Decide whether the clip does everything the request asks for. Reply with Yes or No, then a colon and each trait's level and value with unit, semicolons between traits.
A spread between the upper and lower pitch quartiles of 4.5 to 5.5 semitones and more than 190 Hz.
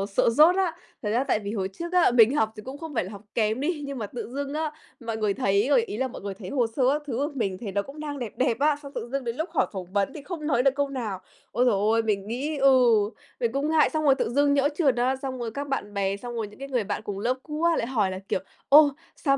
Yes: average, 4.9 semitones; very high, 250 Hz